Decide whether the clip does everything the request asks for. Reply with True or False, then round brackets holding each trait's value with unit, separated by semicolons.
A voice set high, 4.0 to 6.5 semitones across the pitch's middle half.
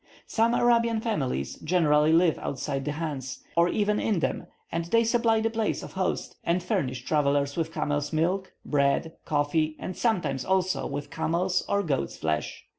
False (165 Hz; 5.2 semitones)